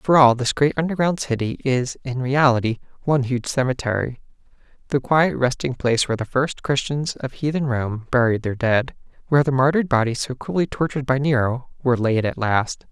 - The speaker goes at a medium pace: Yes, average, 180 wpm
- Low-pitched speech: Yes, low, 130 Hz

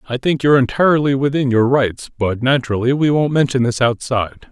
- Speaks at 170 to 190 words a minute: Yes, average, 185 wpm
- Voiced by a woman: No, male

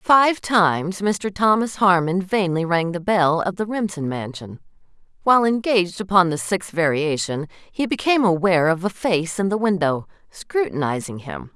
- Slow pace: No, average, 155 wpm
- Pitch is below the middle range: No, medium, 180 Hz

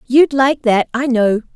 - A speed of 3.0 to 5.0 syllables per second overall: Yes, 4.0 syllables/s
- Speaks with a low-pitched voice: No, very high, 250 Hz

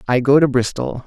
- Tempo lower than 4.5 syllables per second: No, 5.5 syllables/s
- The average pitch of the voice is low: Yes, low, 130 Hz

